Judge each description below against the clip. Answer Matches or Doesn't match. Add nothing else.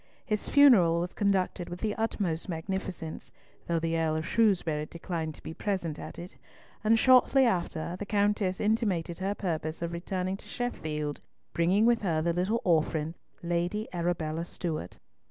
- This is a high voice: Doesn't match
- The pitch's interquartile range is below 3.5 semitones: Doesn't match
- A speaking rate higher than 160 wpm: Doesn't match